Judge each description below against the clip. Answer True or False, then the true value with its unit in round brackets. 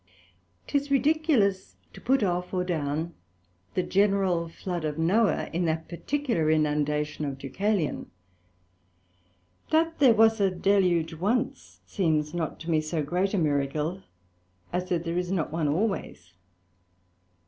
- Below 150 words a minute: True (135 wpm)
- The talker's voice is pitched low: False (175 Hz)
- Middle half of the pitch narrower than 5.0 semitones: True (4.4 semitones)